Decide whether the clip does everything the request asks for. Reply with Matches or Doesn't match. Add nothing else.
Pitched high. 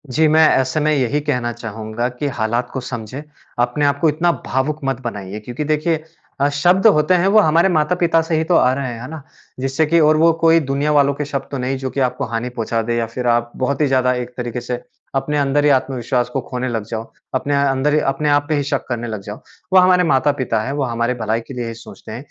Doesn't match